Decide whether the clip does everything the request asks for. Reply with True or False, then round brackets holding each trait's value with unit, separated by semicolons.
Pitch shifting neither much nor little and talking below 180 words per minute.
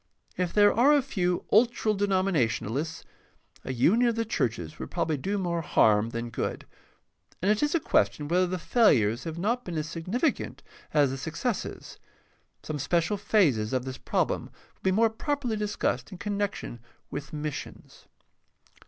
False (6.7 semitones; 160 wpm)